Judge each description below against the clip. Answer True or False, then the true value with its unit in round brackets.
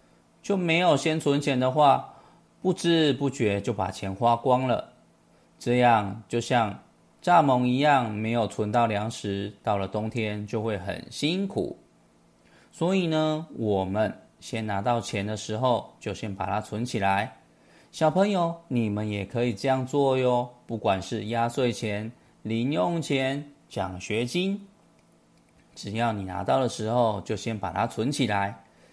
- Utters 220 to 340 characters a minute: False (205 characters per minute)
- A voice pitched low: True (120 Hz)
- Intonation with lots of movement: False (4.8 semitones)